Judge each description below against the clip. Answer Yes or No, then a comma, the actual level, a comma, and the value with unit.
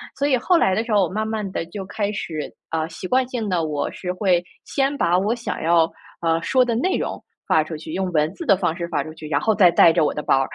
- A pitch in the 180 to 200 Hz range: Yes, medium, 185 Hz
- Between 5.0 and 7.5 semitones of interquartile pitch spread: Yes, average, 5.3 semitones